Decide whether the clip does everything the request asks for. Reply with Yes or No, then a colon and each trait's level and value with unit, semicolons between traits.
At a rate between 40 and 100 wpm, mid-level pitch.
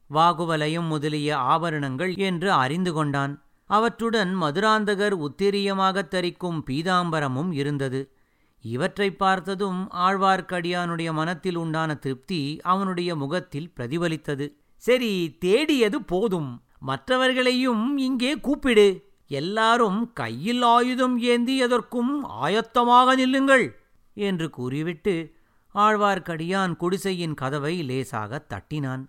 Yes: average, 85 wpm; medium, 180 Hz